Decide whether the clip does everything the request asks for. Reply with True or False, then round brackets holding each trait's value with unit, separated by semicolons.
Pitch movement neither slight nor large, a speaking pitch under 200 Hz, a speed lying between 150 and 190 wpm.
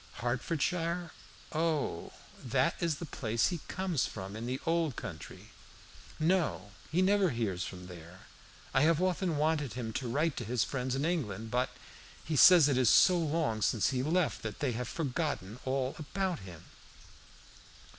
False (6.4 semitones; 135 Hz; 160 wpm)